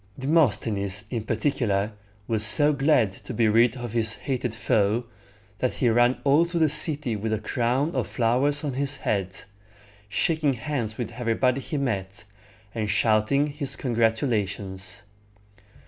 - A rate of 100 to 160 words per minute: Yes, average, 145 wpm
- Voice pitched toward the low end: Yes, low, 120 Hz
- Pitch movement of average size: Yes, average, 4.4 semitones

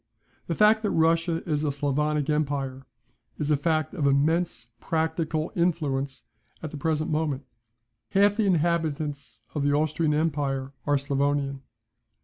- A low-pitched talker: No, medium, 150 Hz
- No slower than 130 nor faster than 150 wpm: Yes, slow, 135 wpm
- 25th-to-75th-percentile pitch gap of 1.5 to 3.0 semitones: Yes, narrow, 2.5 semitones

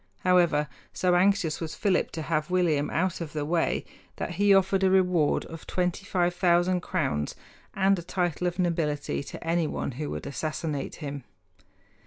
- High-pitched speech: No, medium, 175 Hz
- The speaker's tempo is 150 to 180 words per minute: Yes, average, 155 wpm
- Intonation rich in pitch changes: No, average, 3.0 semitones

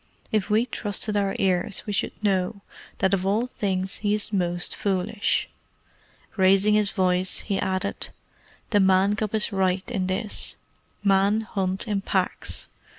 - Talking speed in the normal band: Yes, average, 150 wpm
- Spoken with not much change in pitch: Yes, narrow, 1.8 semitones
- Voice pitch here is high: Yes, high, 195 Hz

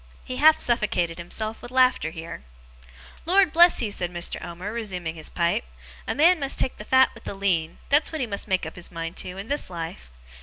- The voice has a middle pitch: No, high, 200 Hz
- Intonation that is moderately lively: No, wide, 7.3 semitones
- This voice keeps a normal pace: No, fast, 215 wpm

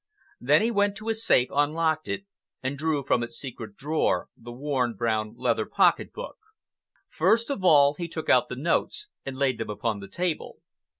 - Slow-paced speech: No, average, 185 wpm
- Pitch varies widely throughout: Yes, wide, 6.2 semitones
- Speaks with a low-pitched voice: No, medium, 145 Hz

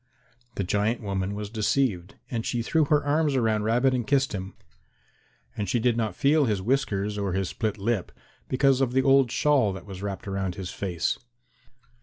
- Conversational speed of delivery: Yes, average, 185 wpm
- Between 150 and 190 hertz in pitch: No, low, 110 Hz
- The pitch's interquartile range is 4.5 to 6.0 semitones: Yes, average, 5.2 semitones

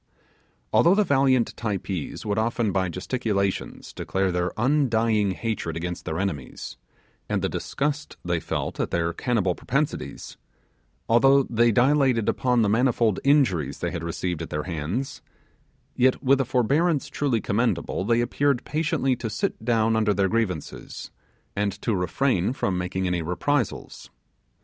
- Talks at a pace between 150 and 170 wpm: No, average, 140 wpm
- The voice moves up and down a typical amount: No, wide, 5.8 semitones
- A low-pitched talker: Yes, low, 110 Hz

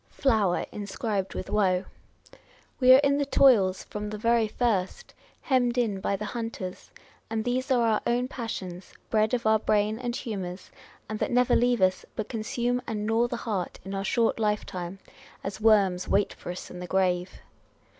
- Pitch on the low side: No, high, 215 Hz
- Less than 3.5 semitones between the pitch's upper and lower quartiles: No, average, 3.8 semitones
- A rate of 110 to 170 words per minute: No, average, 180 wpm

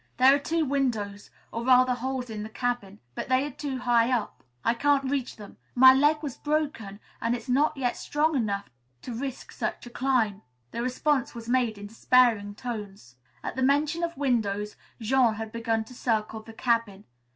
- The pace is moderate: Yes, average, 185 wpm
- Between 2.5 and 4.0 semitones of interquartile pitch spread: Yes, average, 3.5 semitones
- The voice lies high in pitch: Yes, high, 245 Hz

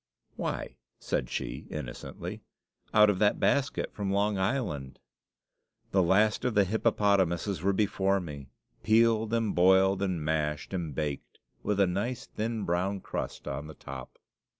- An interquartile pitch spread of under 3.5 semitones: No, average, 3.9 semitones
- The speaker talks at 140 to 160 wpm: Yes, average, 145 wpm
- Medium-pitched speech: No, very low, 95 Hz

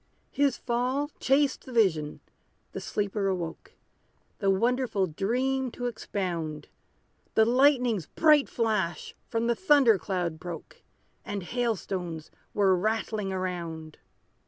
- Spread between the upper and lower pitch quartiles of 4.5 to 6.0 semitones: Yes, wide, 5.6 semitones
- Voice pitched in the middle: No, high, 210 Hz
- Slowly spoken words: Yes, slow, 115 wpm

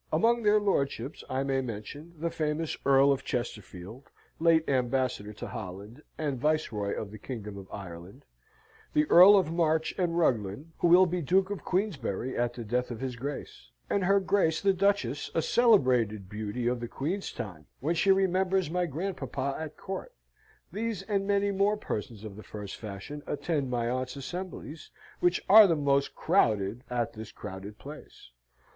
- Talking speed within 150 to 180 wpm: Yes, average, 170 wpm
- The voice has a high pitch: No, medium, 140 Hz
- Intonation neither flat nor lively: No, wide, 7.7 semitones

